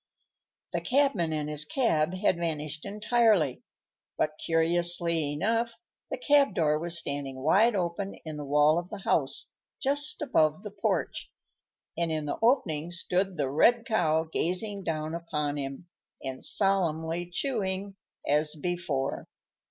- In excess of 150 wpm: No, slow, 135 wpm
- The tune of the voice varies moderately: Yes, average, 4.6 semitones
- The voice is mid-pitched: Yes, medium, 170 Hz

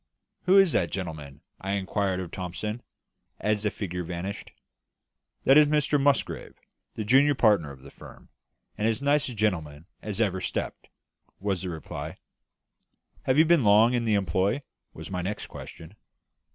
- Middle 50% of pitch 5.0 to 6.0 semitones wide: Yes, wide, 5.6 semitones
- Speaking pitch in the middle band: No, low, 105 Hz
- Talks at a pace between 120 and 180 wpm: Yes, average, 160 wpm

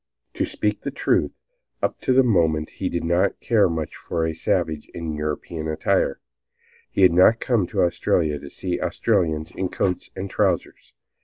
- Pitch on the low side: Yes, very low, 85 Hz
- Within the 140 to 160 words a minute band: No, average, 170 wpm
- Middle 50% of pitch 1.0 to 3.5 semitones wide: Yes, average, 3.2 semitones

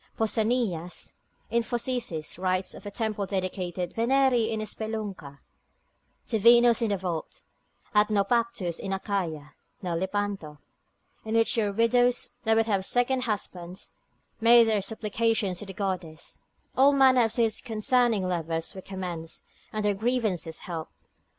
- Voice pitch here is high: Yes, high, 210 Hz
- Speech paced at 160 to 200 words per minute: No, slow, 135 wpm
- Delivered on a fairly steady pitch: No, average, 3.9 semitones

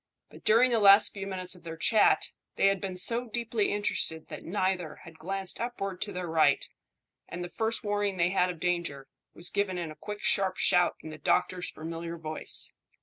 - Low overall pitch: No, medium, 185 Hz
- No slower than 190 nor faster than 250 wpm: Yes, average, 200 wpm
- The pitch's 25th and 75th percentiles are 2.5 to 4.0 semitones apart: Yes, average, 3.3 semitones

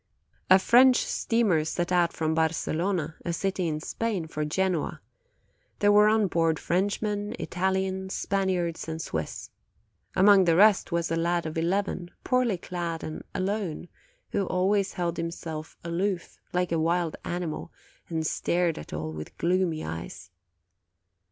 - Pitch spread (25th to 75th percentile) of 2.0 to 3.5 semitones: Yes, average, 3.0 semitones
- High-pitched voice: No, medium, 175 Hz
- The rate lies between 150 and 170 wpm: No, average, 140 wpm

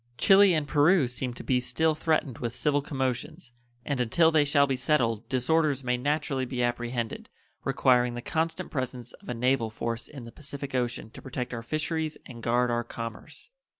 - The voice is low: Yes, low, 130 Hz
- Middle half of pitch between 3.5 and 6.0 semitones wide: Yes, average, 3.8 semitones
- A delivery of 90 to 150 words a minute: No, average, 185 wpm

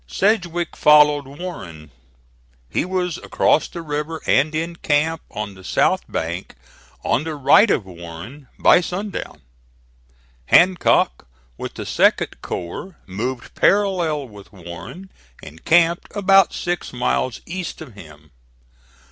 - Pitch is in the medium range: Yes, medium, 150 Hz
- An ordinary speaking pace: No, slow, 120 wpm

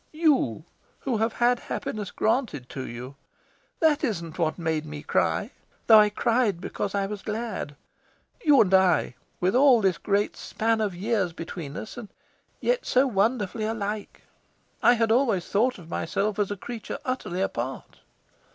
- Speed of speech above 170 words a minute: No, average, 160 wpm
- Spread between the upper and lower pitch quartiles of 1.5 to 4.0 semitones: No, average, 5.1 semitones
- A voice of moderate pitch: No, high, 210 Hz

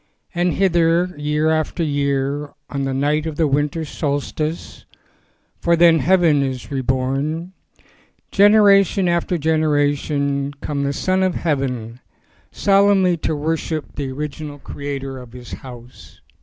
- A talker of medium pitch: Yes, medium, 150 Hz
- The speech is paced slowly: Yes, slow, 125 wpm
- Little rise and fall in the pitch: No, average, 3.4 semitones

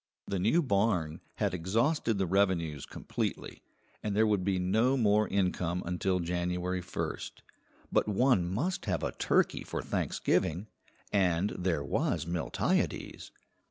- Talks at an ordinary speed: No, slow, 130 wpm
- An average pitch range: Yes, average, 3.1 semitones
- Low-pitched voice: Yes, very low, 95 Hz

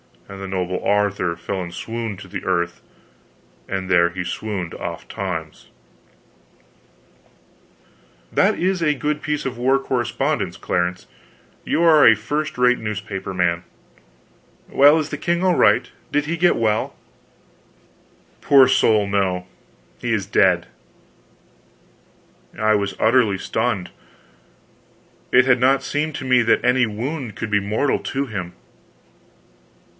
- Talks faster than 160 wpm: No, slow, 135 wpm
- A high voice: No, low, 110 Hz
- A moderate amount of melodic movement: No, wide, 6.0 semitones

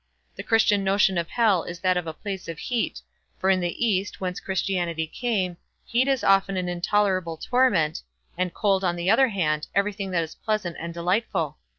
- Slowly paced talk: No, average, 190 wpm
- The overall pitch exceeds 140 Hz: Yes, high, 190 Hz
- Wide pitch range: No, average, 3.1 semitones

